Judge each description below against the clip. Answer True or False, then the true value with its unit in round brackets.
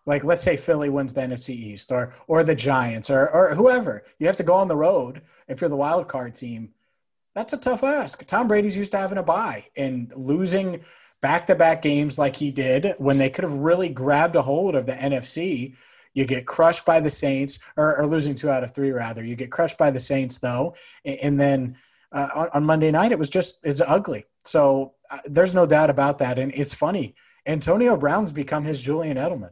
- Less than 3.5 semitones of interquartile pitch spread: False (4.1 semitones)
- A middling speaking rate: False (220 wpm)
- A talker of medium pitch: True (145 Hz)